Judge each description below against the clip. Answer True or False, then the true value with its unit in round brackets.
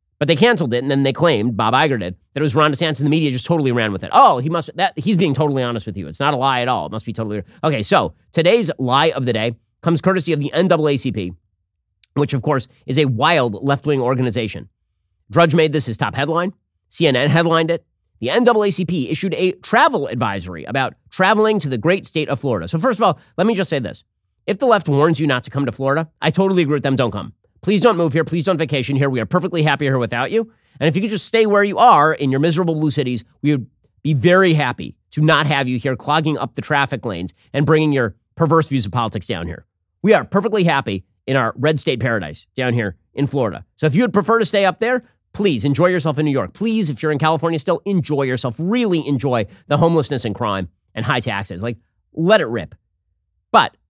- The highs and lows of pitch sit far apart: True (5.8 semitones)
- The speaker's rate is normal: False (240 wpm)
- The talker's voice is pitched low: False (145 Hz)